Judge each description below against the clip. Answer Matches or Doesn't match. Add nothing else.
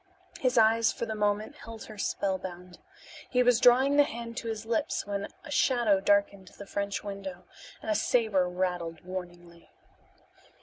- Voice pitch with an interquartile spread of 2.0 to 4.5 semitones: Matches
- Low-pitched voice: Doesn't match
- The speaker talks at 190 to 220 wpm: Doesn't match